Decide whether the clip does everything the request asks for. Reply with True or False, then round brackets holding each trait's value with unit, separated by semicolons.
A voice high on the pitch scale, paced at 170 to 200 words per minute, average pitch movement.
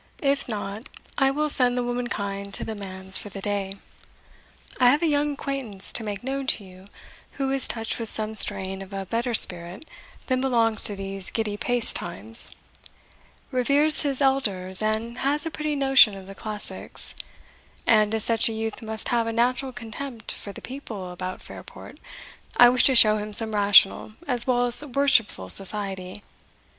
True (225 Hz; 175 wpm; 4.4 semitones)